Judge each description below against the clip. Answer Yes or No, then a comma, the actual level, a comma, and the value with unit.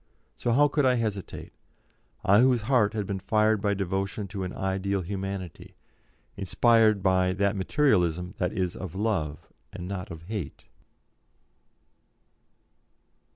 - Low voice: Yes, low, 100 Hz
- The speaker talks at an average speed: No, slow, 130 wpm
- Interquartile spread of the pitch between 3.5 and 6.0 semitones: No, average, 2.8 semitones